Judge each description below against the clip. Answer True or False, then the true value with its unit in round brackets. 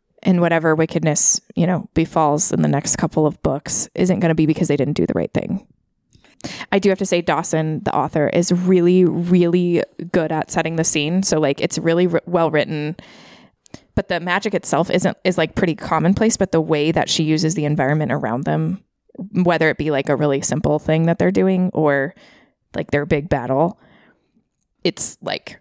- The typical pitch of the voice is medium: True (165 Hz)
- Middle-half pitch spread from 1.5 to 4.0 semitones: True (2.8 semitones)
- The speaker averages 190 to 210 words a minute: True (195 wpm)